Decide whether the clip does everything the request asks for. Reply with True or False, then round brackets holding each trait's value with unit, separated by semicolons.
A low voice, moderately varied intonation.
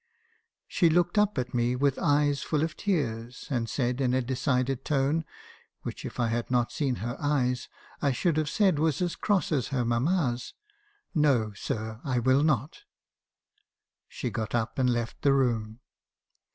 True (130 Hz; 3.8 semitones)